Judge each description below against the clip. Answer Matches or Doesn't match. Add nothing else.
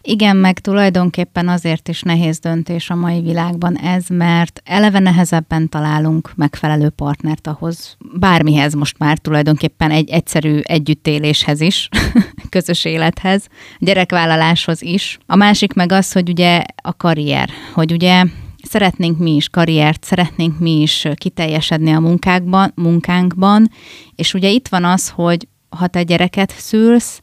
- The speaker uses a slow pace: Doesn't match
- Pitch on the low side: Doesn't match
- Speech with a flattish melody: Matches